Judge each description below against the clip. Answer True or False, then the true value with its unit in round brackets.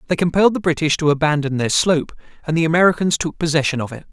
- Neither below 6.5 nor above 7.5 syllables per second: True (7.0 syllables/s)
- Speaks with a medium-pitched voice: True (160 Hz)